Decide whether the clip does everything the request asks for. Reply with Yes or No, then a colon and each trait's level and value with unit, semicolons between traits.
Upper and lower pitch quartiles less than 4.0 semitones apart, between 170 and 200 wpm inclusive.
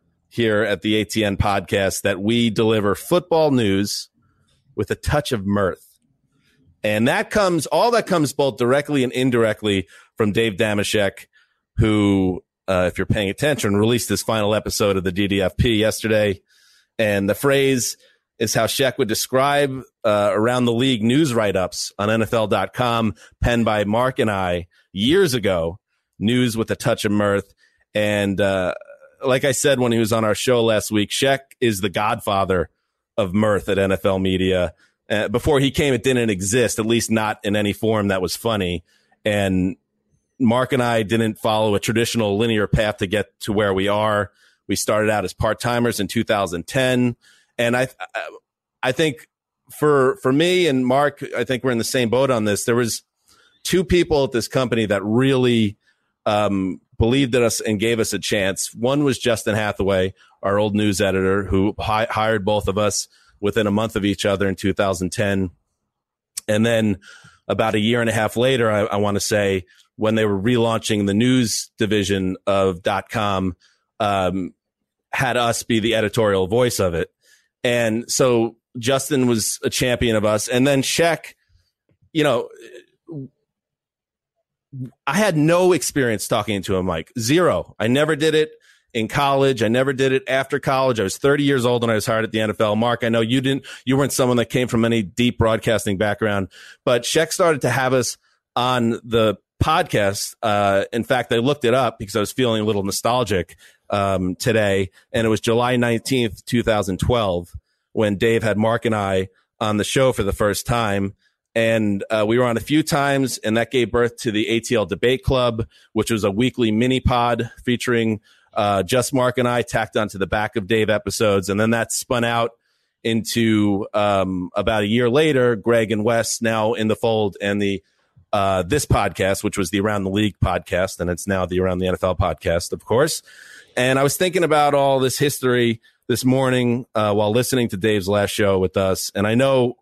Yes: average, 3.6 semitones; average, 185 wpm